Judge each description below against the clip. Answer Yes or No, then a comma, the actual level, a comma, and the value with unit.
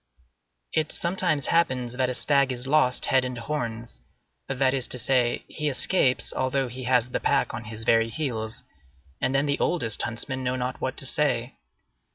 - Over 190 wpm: No, average, 180 wpm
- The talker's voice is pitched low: Yes, low, 130 Hz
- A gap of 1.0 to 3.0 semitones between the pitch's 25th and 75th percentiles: Yes, narrow, 2.4 semitones